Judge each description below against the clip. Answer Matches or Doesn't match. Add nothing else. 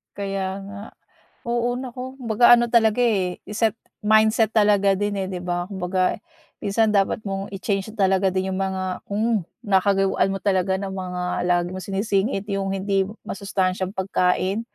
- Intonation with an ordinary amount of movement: Doesn't match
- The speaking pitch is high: Matches